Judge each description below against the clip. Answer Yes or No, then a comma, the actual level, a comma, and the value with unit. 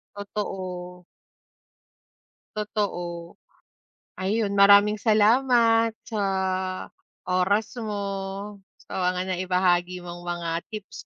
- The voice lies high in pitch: Yes, high, 195 Hz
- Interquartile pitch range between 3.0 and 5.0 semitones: No, narrow, 2.6 semitones